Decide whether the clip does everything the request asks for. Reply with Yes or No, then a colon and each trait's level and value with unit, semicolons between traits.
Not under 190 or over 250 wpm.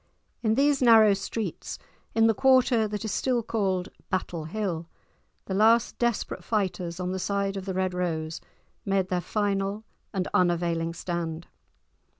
No: average, 150 wpm